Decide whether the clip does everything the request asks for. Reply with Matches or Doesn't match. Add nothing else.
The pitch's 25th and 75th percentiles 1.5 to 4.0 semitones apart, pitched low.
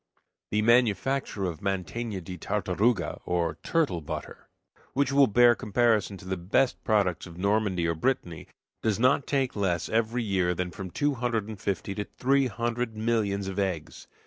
Doesn't match